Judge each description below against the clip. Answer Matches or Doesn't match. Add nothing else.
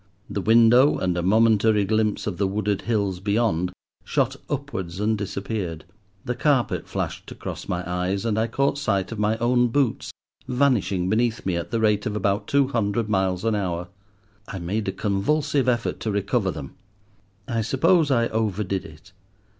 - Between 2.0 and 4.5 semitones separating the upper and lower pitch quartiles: Matches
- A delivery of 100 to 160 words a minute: Doesn't match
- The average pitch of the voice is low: Matches